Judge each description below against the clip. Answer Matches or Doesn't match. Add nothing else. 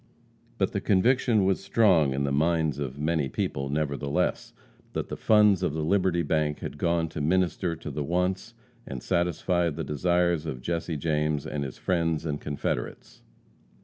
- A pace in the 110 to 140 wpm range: Doesn't match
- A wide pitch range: Doesn't match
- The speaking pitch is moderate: Doesn't match